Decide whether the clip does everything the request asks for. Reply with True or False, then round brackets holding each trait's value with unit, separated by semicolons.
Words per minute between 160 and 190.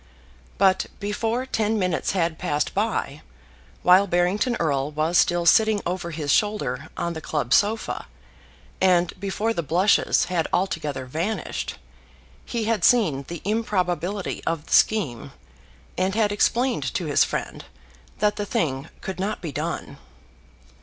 False (140 wpm)